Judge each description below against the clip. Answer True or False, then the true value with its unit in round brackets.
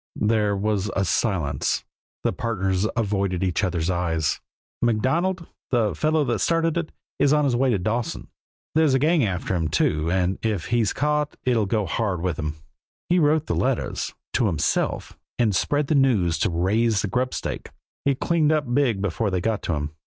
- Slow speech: False (180 wpm)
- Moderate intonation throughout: False (6.4 semitones)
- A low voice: True (110 Hz)